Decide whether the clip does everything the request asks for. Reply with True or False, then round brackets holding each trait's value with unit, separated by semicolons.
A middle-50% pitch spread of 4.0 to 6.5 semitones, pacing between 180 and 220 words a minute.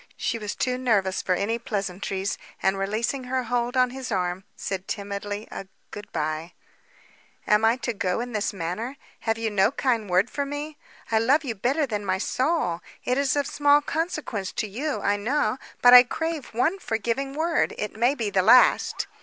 True (4.9 semitones; 185 wpm)